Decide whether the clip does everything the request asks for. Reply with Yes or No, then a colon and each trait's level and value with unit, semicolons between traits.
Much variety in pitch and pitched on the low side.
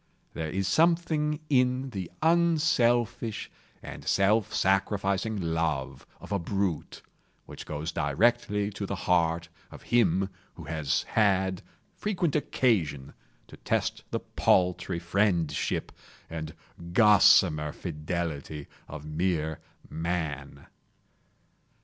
Yes: wide, 5.7 semitones; very low, 95 Hz